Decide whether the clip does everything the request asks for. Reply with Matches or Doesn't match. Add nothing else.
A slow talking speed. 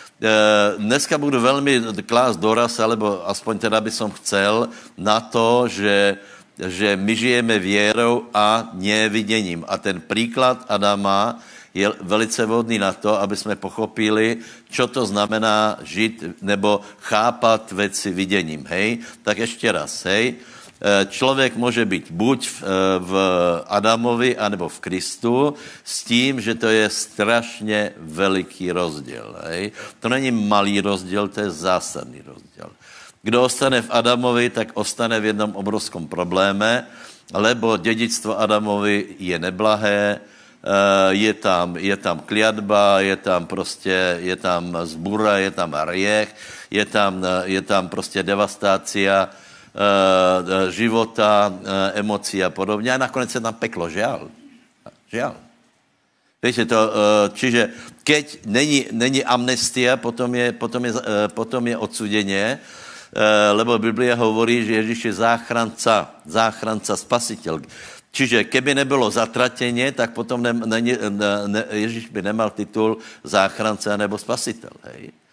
Doesn't match